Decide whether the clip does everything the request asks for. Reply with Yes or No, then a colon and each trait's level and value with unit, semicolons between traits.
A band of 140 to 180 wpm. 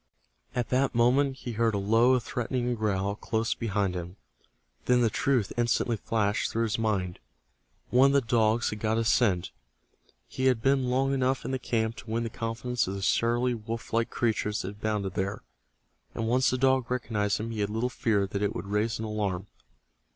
No: average, 195 wpm